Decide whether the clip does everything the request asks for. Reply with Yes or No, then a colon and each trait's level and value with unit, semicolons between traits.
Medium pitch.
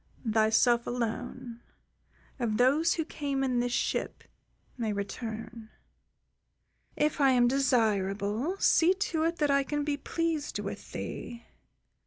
No: very high, 250 Hz